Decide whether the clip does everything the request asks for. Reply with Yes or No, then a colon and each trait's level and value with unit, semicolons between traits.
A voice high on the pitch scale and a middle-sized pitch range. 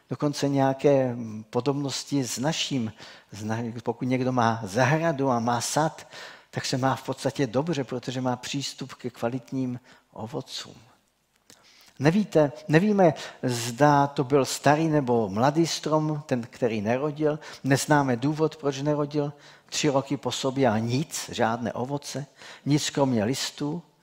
No: low, 135 Hz; average, 3.0 semitones